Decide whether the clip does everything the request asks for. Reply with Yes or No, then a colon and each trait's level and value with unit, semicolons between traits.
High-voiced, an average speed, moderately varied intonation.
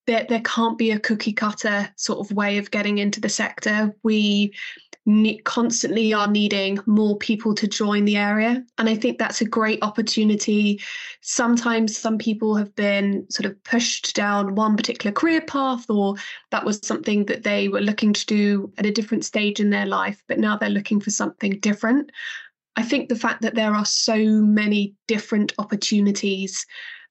No: high, 215 Hz; average, 180 wpm; narrow, 1.8 semitones